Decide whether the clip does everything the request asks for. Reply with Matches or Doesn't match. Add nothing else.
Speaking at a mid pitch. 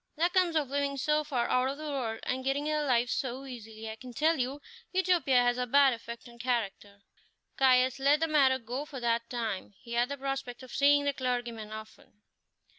Doesn't match